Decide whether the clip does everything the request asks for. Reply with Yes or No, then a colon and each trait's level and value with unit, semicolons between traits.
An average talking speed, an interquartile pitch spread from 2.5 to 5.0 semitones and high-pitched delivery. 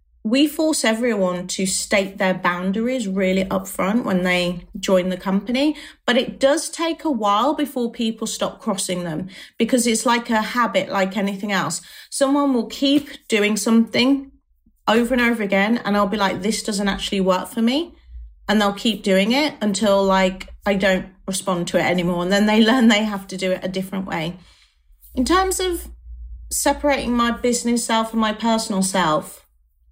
Yes: average, 175 wpm; average, 4.3 semitones; high, 210 Hz